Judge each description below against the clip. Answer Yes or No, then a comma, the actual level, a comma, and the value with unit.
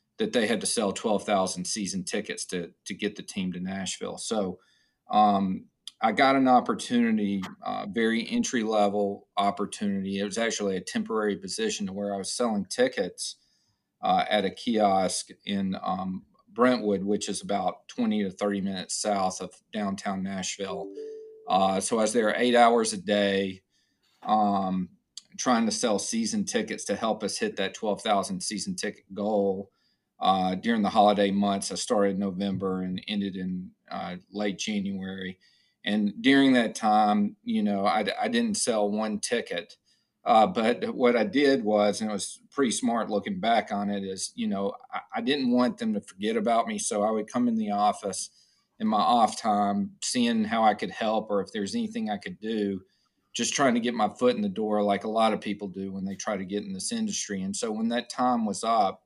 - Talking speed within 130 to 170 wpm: No, average, 190 wpm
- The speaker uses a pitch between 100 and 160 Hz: Yes, low, 105 Hz